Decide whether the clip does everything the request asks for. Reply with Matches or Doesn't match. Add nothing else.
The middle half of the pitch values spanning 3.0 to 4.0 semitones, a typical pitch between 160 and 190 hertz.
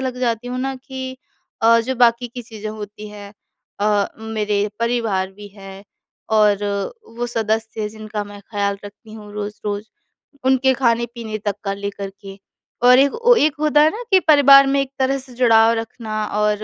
Doesn't match